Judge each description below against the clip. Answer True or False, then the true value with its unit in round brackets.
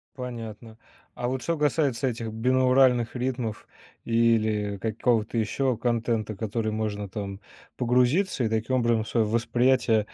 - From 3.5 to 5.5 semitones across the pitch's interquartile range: False (2.5 semitones)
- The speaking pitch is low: True (115 Hz)